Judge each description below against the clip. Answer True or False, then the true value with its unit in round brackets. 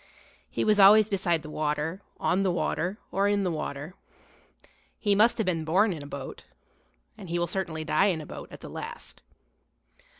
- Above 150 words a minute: True (190 wpm)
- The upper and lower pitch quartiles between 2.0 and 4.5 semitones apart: True (4.2 semitones)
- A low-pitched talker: False (180 Hz)